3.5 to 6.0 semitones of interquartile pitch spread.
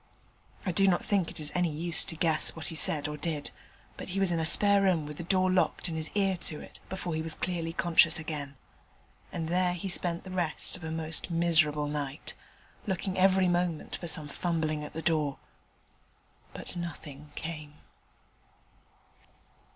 No: narrow, 2.6 semitones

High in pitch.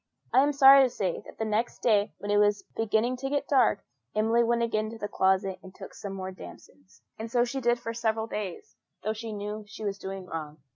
Yes: high, 215 Hz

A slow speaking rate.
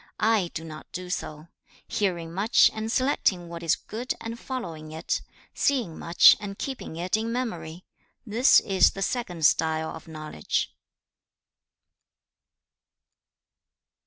Yes: slow, 125 wpm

